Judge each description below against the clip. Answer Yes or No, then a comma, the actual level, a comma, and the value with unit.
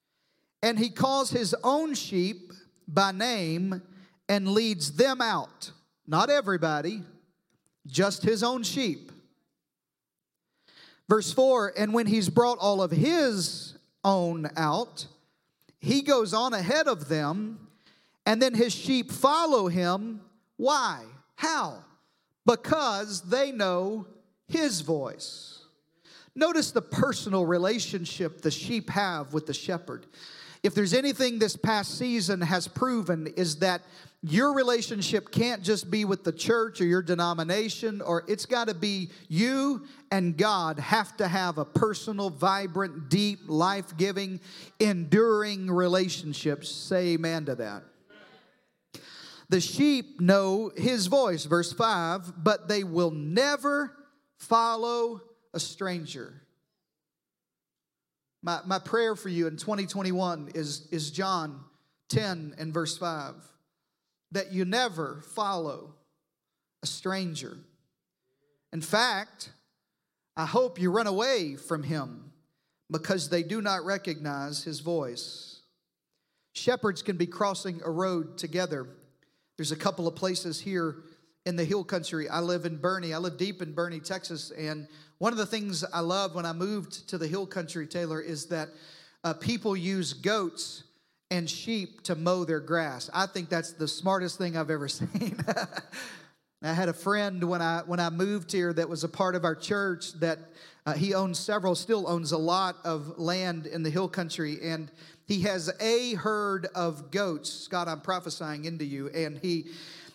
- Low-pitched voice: No, medium, 180 Hz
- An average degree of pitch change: Yes, average, 4.2 semitones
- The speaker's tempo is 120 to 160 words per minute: Yes, average, 140 wpm